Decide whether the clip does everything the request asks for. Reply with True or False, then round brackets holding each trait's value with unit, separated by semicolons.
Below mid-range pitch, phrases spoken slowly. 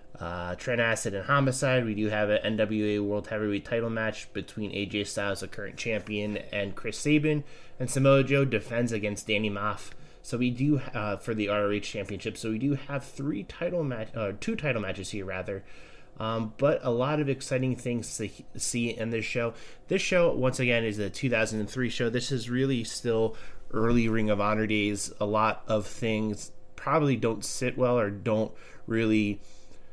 False (110 Hz; 185 wpm)